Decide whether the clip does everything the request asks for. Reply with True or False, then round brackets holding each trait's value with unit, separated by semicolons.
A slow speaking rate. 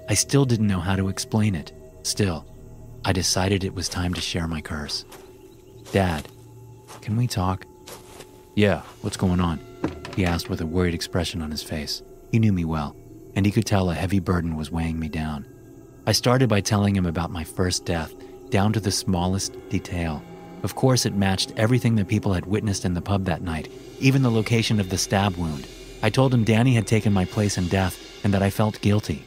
False (205 wpm)